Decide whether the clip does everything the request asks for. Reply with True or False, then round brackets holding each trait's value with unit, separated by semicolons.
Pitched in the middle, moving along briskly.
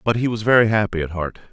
False (105 Hz; 275 wpm)